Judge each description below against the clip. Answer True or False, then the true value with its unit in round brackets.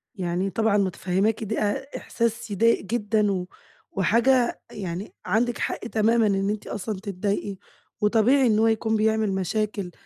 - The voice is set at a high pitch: True (215 Hz)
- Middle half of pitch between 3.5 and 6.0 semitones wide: False (2.5 semitones)